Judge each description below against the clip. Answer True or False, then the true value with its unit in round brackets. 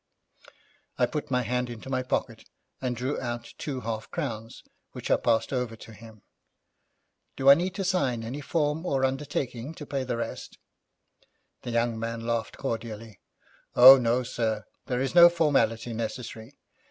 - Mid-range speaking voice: False (125 Hz)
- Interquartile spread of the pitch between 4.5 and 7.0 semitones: False (3.2 semitones)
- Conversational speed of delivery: True (160 wpm)